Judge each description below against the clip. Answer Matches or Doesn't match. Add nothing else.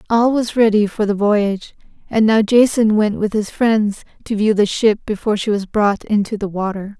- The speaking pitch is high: Matches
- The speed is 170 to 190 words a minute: Doesn't match